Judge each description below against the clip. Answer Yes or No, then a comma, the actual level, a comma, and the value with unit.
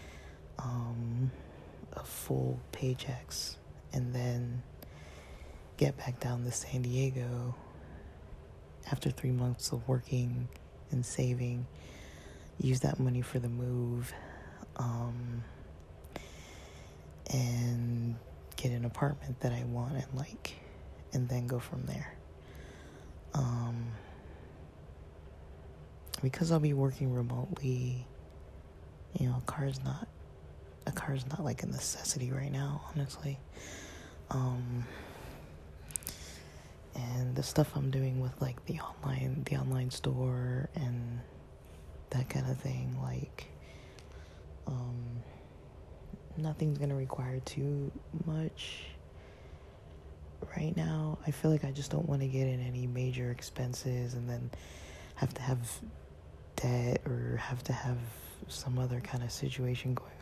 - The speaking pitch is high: No, low, 120 Hz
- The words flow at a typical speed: No, slow, 115 wpm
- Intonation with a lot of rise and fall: Yes, wide, 8.8 semitones